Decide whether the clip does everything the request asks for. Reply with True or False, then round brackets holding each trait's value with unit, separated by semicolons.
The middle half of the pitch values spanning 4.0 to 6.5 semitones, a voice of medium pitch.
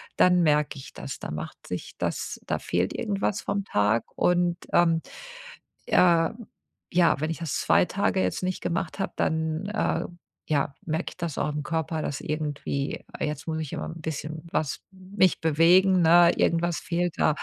False (2.8 semitones; 165 Hz)